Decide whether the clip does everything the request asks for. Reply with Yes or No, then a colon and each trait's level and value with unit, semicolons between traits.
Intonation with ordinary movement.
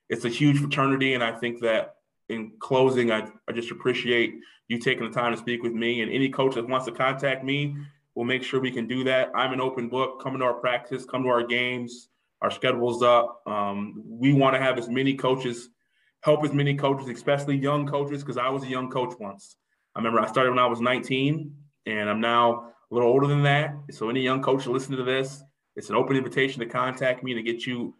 No: narrow, 2.1 semitones